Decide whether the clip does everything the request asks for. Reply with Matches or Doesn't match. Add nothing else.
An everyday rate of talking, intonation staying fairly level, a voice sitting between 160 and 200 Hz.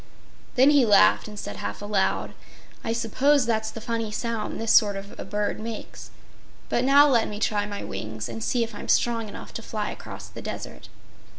Doesn't match